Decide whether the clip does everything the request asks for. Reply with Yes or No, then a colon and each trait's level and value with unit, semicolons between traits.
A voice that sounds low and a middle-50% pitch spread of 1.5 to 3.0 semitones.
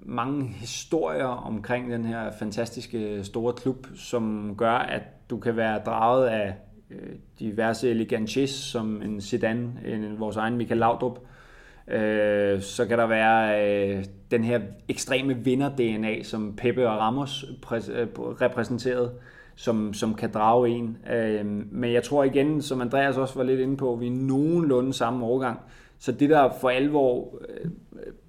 Yes: low, 120 Hz; average, 2.7 semitones